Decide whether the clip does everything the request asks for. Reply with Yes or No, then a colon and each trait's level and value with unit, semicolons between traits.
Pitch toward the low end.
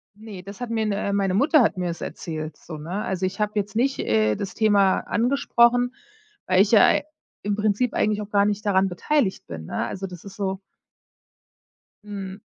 No: high, 200 Hz